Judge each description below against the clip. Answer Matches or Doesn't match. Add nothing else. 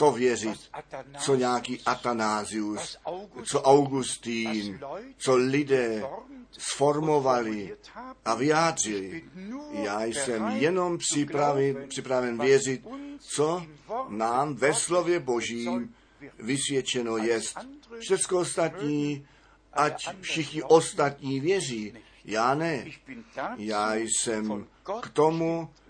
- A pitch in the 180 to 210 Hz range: Doesn't match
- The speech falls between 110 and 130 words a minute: Doesn't match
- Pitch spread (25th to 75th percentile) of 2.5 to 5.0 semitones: Doesn't match